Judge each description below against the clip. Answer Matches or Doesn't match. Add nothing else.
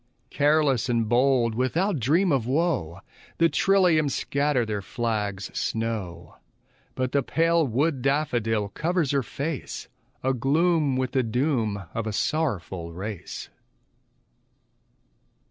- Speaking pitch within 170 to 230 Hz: Doesn't match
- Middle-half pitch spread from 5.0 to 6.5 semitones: Matches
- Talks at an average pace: Doesn't match